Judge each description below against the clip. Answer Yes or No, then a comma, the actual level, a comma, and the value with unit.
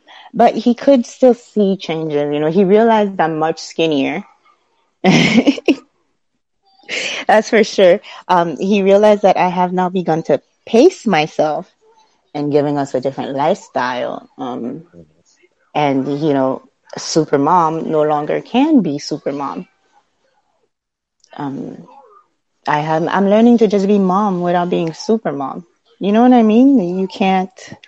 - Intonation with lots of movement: Yes, wide, 7.2 semitones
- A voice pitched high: Yes, high, 195 Hz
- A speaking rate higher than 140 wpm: No, slow, 135 wpm